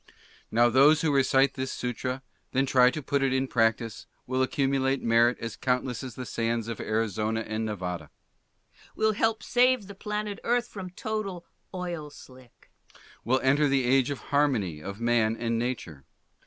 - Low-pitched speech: Yes, low, 130 Hz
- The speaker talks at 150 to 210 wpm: Yes, average, 170 wpm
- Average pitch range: Yes, average, 4.3 semitones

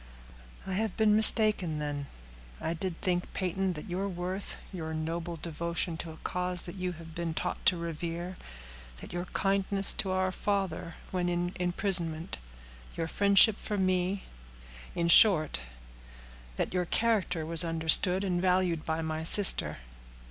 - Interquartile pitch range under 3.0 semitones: Yes, narrow, 2.5 semitones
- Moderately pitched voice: Yes, medium, 175 Hz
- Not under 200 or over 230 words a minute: No, average, 145 wpm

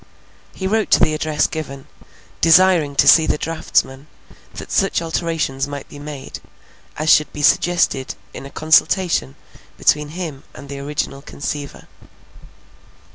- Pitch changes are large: No, average, 2.8 semitones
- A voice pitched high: No, medium, 150 Hz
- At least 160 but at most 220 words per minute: No, slow, 135 wpm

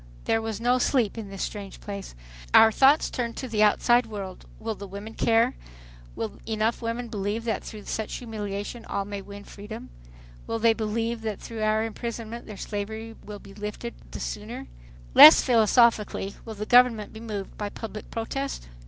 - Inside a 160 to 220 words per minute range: Yes, average, 175 wpm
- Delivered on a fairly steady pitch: Yes, narrow, 2.0 semitones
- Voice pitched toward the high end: Yes, high, 220 Hz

